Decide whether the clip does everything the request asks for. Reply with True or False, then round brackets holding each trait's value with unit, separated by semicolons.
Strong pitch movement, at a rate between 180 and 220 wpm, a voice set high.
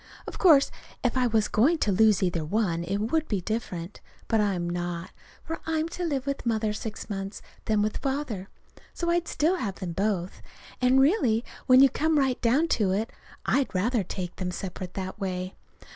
True (6.2 semitones; 190 wpm; 220 Hz)